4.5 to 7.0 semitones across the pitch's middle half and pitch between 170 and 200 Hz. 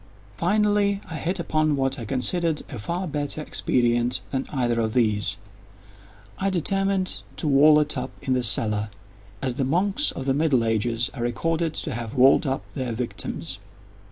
No: wide, 5.6 semitones; low, 135 Hz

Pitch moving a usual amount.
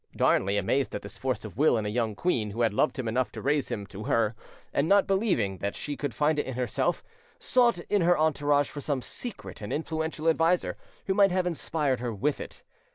No: wide, 6.2 semitones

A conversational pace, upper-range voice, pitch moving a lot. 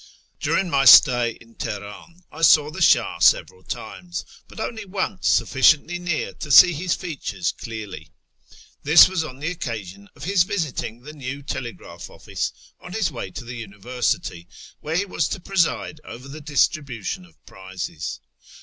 No: average, 160 wpm; medium, 140 Hz; wide, 7.0 semitones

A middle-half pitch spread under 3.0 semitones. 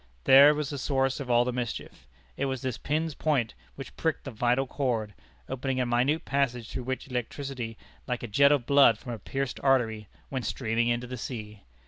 Yes: narrow, 2.5 semitones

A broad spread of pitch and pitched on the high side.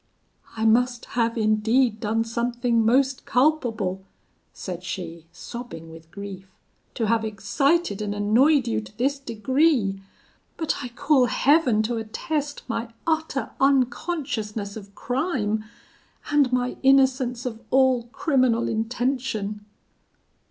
No: average, 3.9 semitones; high, 235 Hz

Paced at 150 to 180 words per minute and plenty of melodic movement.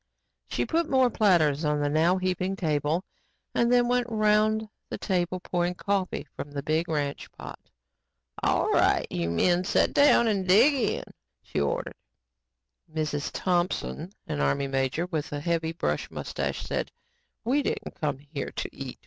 Yes: average, 160 wpm; wide, 6.2 semitones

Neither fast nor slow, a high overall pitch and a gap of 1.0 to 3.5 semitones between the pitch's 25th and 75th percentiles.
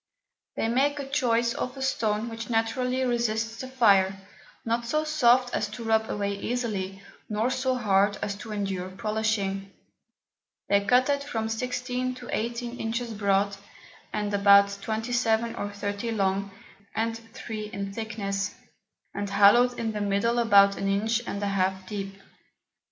Yes: average, 150 wpm; high, 220 Hz; average, 3.1 semitones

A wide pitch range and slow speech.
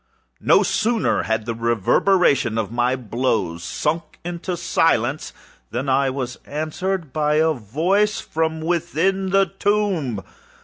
Yes: wide, 6.6 semitones; slow, 125 wpm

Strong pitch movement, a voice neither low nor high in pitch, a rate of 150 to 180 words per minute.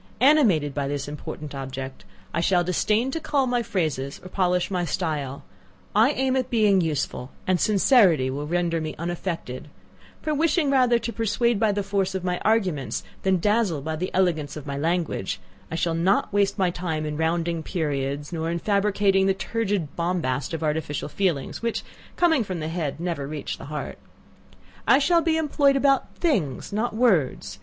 Yes: wide, 6.1 semitones; medium, 180 Hz; average, 175 wpm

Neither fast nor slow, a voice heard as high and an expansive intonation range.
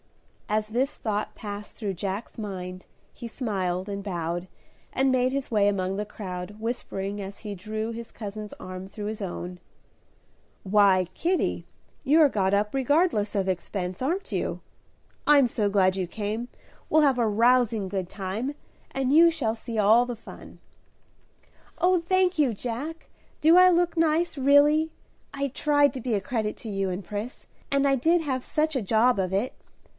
Yes: average, 170 wpm; high, 220 Hz; wide, 5.8 semitones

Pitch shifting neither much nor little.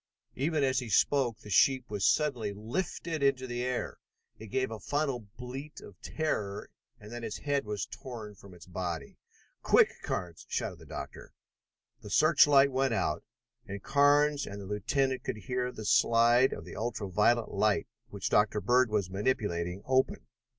Yes: average, 4.4 semitones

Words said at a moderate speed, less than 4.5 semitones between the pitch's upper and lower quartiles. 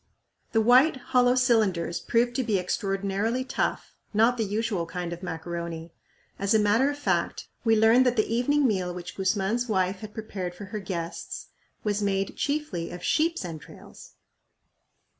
No: average, 160 wpm; average, 4.8 semitones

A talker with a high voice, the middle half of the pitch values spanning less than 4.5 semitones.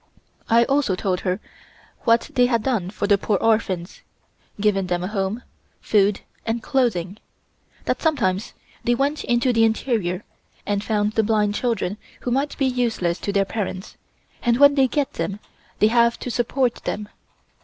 Yes: high, 220 Hz; average, 3.7 semitones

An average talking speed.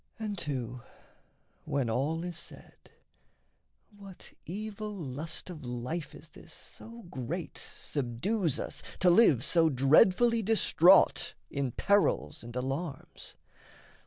No: slow, 110 wpm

